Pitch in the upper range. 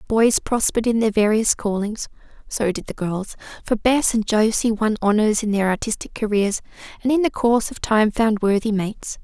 Yes: high, 215 Hz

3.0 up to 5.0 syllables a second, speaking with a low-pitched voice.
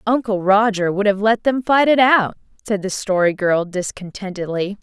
No: 4.8 syllables/s; high, 205 Hz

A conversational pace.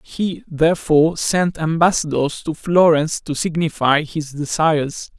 No: slow, 115 wpm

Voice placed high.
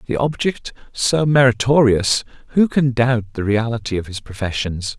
No: low, 120 Hz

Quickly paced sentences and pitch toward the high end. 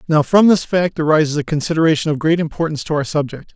No: fast, 220 wpm; medium, 155 Hz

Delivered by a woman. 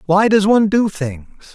No: male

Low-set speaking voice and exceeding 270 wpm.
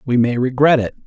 No: low, 130 Hz; fast, 225 wpm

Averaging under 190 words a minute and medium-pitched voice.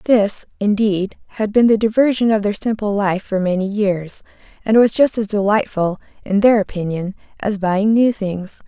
No: average, 175 wpm; high, 205 Hz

